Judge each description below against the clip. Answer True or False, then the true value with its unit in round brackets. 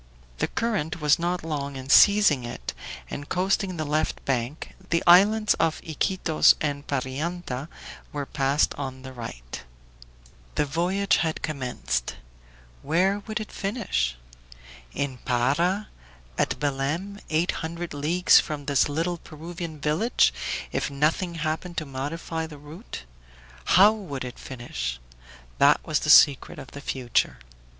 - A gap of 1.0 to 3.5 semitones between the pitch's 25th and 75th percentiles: False (4.4 semitones)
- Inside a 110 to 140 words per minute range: True (135 wpm)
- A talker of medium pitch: True (155 Hz)